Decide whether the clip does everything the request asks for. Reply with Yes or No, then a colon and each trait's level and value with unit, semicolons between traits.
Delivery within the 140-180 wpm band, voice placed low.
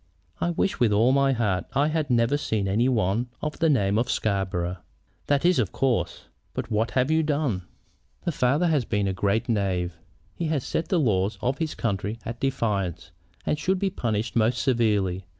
No: average, 190 wpm; low, 115 Hz